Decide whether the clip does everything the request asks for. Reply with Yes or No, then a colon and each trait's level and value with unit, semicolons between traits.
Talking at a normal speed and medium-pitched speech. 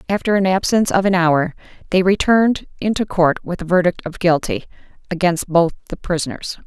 Yes: average, 170 wpm; medium, 180 Hz